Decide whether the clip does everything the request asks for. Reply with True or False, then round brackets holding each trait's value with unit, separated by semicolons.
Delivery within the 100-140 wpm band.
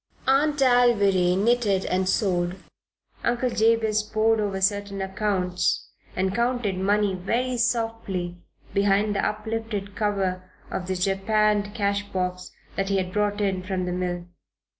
True (135 wpm)